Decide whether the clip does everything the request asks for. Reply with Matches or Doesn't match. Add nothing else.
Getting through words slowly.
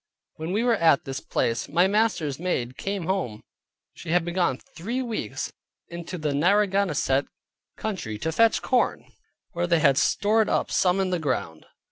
Doesn't match